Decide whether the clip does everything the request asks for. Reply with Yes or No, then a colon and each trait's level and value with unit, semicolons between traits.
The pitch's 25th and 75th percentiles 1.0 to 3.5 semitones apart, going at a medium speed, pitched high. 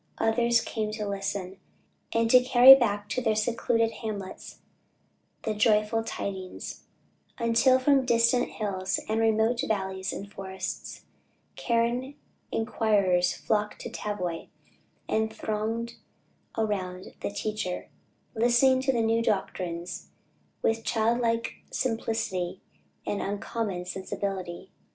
No: average, 3.0 semitones; slow, 110 wpm; high, 220 Hz